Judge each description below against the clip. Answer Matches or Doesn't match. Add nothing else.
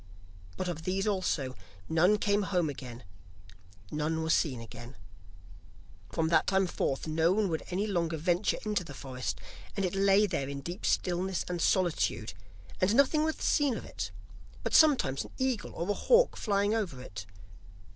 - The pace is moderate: Matches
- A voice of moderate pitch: Matches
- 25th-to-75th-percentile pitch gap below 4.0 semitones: Doesn't match